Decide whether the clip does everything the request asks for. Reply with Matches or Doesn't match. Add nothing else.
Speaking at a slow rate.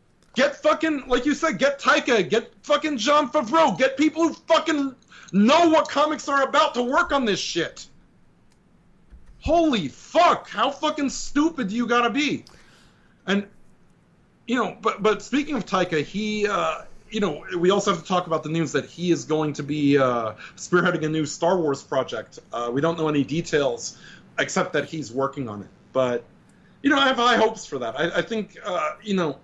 Doesn't match